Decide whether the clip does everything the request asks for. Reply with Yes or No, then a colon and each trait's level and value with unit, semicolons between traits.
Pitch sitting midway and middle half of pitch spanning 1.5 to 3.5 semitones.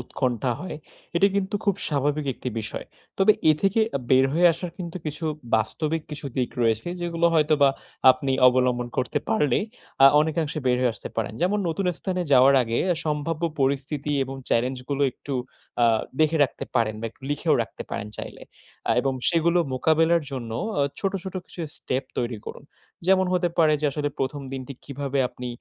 No: medium, 145 Hz; average, 4.4 semitones